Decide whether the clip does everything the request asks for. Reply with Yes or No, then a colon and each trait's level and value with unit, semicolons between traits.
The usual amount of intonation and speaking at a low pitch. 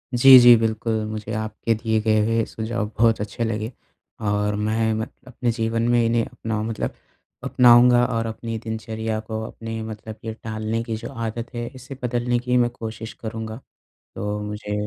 No: narrow, 1.3 semitones; low, 115 Hz